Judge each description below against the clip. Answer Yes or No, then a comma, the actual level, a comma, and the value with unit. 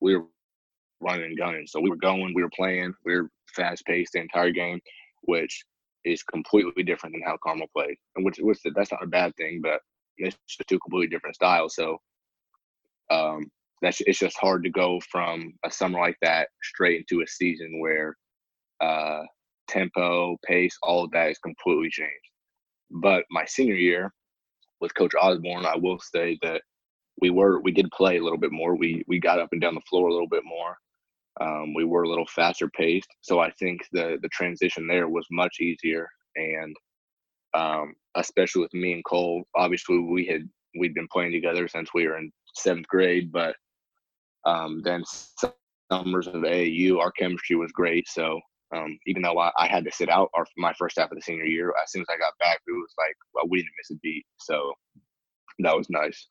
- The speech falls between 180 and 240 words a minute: Yes, average, 195 wpm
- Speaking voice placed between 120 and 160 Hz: No, very low, 85 Hz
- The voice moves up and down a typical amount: No, narrow, 1.5 semitones